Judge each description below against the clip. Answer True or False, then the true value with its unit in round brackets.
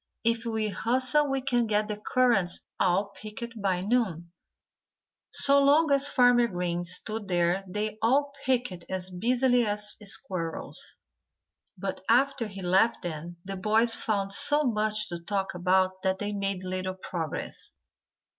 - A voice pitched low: False (210 Hz)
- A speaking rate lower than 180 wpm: True (145 wpm)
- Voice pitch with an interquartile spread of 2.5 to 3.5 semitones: False (4.4 semitones)